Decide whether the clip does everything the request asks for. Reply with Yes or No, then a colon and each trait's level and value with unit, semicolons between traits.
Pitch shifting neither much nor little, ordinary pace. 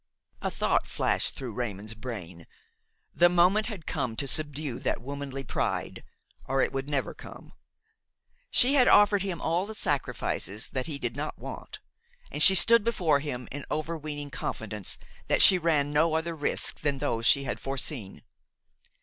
Yes: average, 4.9 semitones; average, 160 wpm